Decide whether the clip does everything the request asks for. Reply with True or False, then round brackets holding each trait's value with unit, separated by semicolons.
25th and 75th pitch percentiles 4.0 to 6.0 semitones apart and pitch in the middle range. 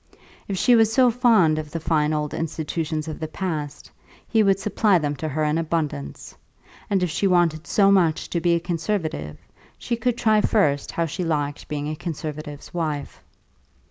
True (4.3 semitones; 165 Hz)